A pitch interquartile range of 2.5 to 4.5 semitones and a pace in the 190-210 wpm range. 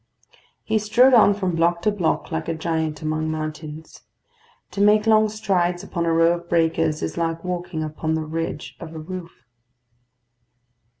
No: average, 2.9 semitones; average, 165 wpm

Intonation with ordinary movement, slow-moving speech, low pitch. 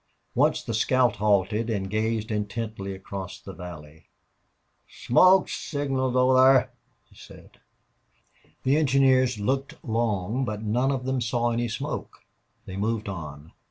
Yes: average, 4.2 semitones; slow, 130 wpm; low, 115 Hz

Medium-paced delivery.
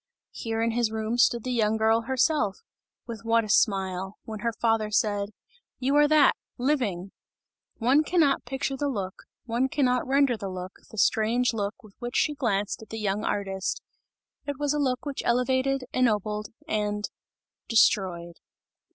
Yes: average, 160 wpm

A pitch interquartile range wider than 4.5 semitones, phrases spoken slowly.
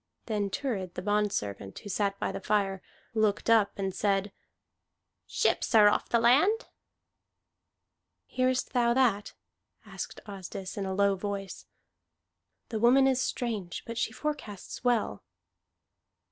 No: average, 3.5 semitones; slow, 130 wpm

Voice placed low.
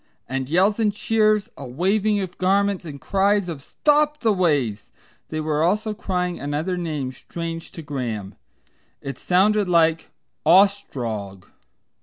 No: medium, 175 Hz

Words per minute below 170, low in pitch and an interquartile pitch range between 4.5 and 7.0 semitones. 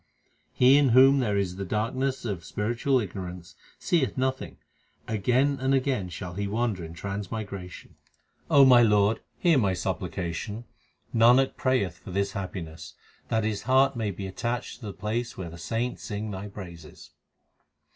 Yes: average, 155 wpm; low, 105 Hz; average, 4.9 semitones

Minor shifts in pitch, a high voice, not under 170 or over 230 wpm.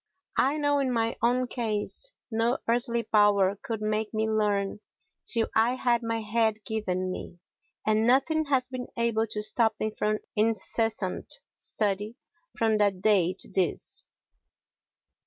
No: narrow, 2.1 semitones; high, 220 Hz; average, 140 wpm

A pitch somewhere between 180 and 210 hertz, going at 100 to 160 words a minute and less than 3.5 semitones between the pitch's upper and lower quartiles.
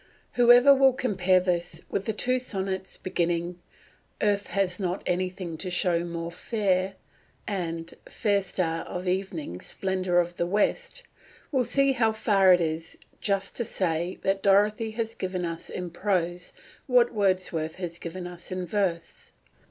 Yes: medium, 185 Hz; average, 150 wpm; average, 2.9 semitones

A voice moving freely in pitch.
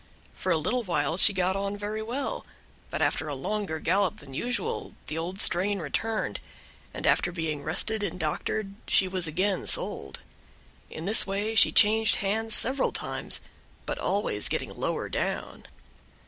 No: average, 4.7 semitones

